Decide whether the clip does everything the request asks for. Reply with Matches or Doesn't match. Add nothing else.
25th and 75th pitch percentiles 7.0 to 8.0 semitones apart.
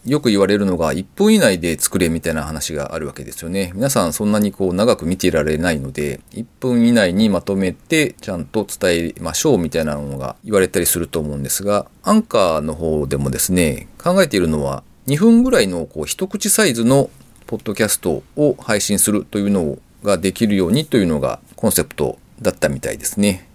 Doesn't match